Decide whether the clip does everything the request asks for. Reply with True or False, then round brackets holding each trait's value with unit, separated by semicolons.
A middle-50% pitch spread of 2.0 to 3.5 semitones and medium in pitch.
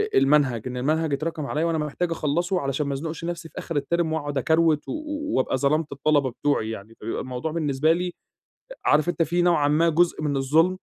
True (3.1 semitones; 150 Hz)